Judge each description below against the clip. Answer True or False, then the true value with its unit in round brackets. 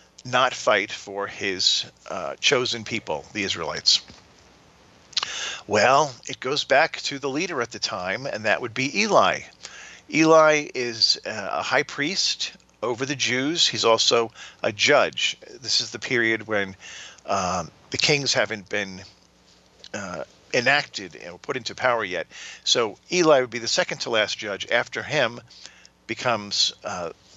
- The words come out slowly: False (145 wpm)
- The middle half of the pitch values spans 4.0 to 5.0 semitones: True (4.5 semitones)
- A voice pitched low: True (115 Hz)